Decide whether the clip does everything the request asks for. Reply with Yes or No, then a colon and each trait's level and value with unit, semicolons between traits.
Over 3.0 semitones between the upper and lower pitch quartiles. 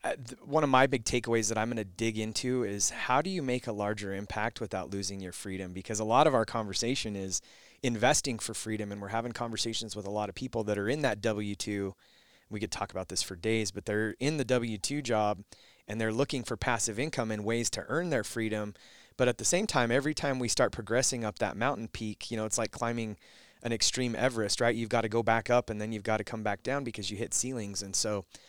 No: average, 2.7 semitones